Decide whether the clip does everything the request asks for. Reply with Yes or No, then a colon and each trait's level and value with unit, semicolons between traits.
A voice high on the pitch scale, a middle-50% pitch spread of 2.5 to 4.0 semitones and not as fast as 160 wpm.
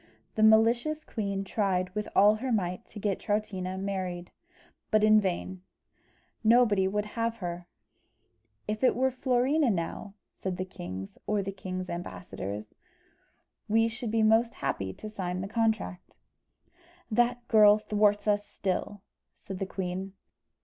Yes: high, 205 Hz; average, 3.1 semitones; average, 140 wpm